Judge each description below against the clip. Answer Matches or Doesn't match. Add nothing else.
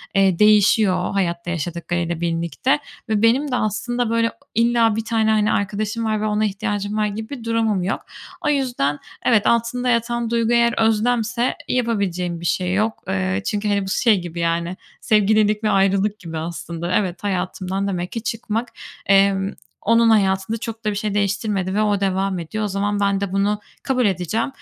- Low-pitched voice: Doesn't match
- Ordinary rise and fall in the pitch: Matches